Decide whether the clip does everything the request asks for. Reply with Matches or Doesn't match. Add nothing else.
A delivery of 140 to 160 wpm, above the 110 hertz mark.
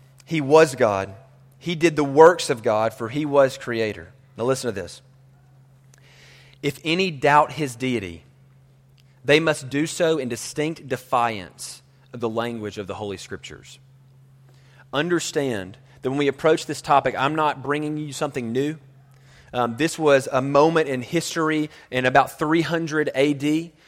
Matches